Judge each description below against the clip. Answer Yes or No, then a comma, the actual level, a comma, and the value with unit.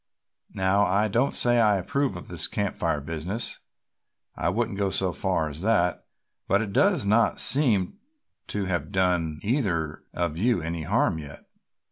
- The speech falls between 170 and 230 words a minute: No, average, 160 wpm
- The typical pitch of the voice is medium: No, very low, 95 Hz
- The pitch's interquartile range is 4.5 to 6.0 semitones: Yes, average, 4.8 semitones